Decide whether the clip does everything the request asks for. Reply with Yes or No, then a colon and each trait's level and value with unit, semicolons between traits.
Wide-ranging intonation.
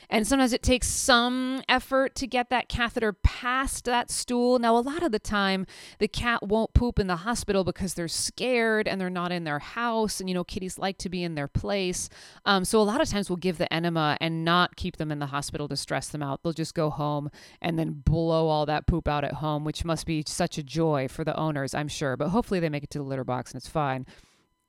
Yes: wide, 6.6 semitones